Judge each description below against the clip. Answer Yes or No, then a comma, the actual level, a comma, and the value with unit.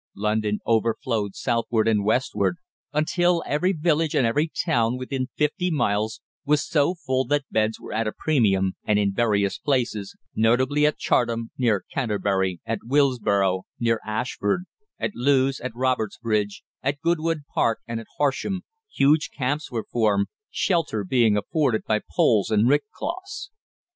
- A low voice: Yes, low, 120 Hz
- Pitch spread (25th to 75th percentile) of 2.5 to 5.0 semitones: No, wide, 5.5 semitones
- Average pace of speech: Yes, average, 145 wpm